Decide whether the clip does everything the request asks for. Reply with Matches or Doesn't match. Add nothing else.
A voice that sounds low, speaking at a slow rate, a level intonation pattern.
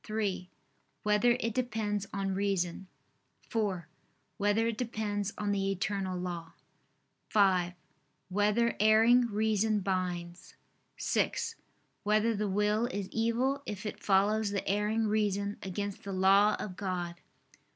Doesn't match